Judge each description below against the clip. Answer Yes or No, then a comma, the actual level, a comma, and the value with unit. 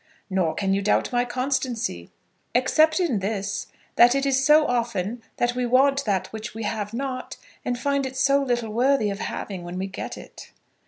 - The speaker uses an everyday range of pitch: Yes, average, 4.6 semitones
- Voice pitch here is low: No, high, 245 Hz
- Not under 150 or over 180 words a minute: No, average, 190 wpm